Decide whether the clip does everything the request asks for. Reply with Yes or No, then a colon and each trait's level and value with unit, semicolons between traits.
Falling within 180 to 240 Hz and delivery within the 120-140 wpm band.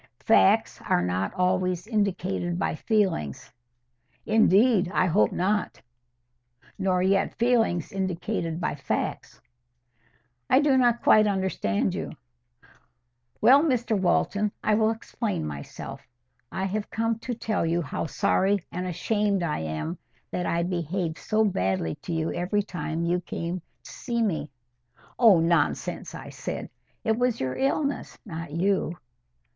Yes: high, 190 Hz; slow, 135 wpm